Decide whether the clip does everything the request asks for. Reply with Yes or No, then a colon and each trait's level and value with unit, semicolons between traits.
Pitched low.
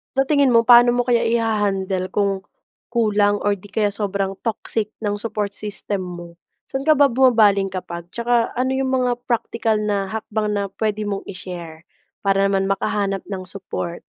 No: high, 205 Hz